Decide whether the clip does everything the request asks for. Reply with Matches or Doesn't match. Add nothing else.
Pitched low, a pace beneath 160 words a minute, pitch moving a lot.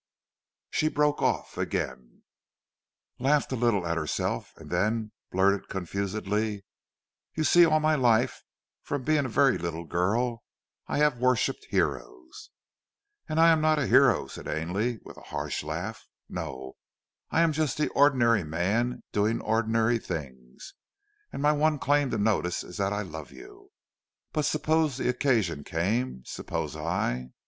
Matches